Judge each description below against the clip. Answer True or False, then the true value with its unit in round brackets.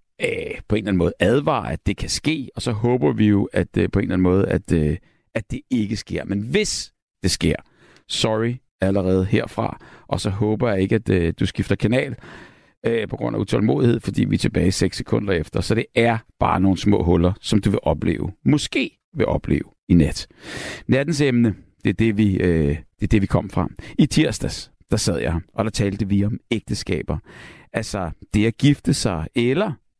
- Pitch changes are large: False (3.7 semitones)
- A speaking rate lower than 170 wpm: False (210 wpm)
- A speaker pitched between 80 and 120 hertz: True (105 Hz)